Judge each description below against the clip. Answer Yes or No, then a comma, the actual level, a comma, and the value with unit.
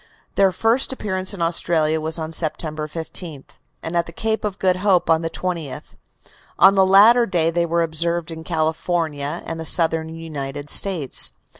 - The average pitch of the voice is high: No, medium, 165 Hz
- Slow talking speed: No, average, 170 wpm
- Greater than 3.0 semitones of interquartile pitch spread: No, average, 2.7 semitones